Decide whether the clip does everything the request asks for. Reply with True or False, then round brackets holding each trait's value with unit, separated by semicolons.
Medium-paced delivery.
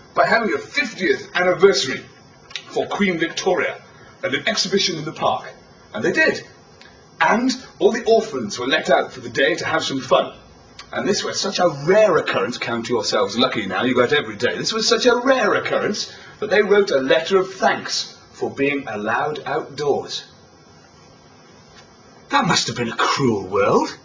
True (175 wpm)